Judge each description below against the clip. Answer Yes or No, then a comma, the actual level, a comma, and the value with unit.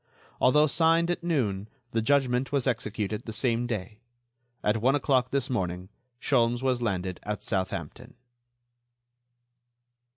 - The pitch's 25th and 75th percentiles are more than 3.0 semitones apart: Yes, average, 4.3 semitones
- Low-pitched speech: Yes, low, 120 Hz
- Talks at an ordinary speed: No, slow, 125 wpm